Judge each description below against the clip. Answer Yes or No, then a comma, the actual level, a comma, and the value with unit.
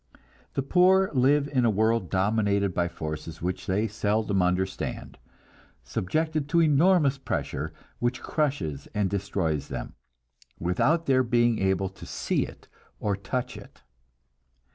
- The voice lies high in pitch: No, low, 110 Hz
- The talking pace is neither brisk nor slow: No, slow, 130 wpm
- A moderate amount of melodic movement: No, wide, 6.6 semitones